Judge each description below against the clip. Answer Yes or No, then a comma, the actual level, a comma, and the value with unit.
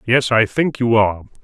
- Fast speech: Yes, fast, 210 wpm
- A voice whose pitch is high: No, low, 115 Hz